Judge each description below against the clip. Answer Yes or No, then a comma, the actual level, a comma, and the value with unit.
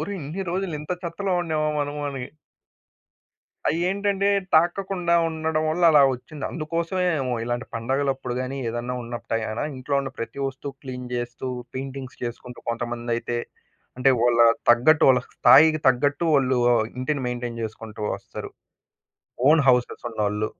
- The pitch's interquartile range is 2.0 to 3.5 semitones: No, average, 4.6 semitones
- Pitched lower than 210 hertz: Yes, low, 135 Hz